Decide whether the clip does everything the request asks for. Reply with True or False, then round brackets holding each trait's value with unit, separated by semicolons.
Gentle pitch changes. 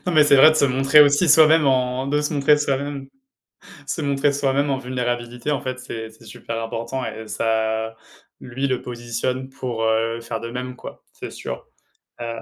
False (3.3 semitones)